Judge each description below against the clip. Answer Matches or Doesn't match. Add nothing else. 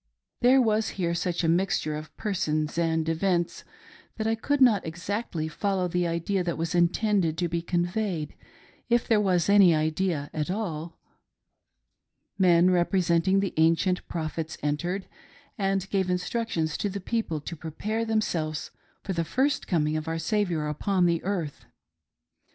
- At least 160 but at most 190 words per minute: Doesn't match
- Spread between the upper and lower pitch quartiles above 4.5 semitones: Doesn't match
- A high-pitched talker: Doesn't match